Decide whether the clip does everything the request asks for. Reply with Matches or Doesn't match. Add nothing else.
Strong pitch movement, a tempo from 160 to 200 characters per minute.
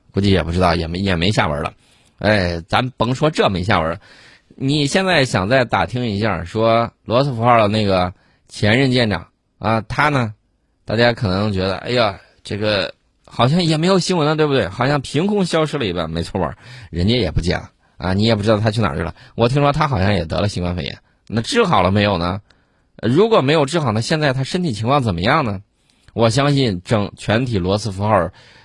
Doesn't match